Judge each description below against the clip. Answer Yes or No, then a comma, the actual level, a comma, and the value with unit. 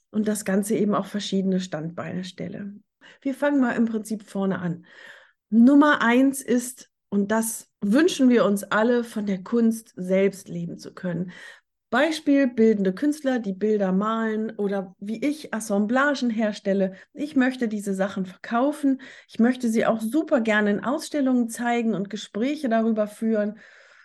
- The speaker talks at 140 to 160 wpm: Yes, average, 150 wpm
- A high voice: Yes, high, 220 Hz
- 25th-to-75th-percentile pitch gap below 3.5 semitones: No, average, 3.8 semitones